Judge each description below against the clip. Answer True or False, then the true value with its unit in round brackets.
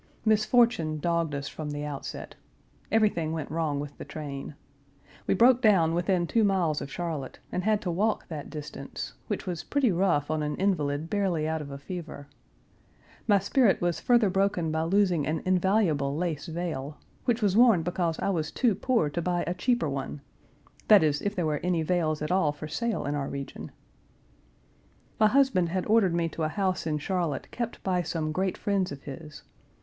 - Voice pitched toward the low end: False (170 Hz)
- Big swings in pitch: False (4.5 semitones)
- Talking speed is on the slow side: False (185 wpm)